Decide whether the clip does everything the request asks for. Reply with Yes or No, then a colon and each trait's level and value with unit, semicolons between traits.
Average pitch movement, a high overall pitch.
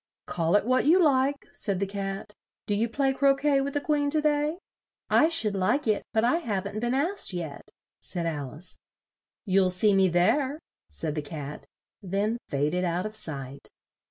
No: wide, 7.5 semitones; high, 210 Hz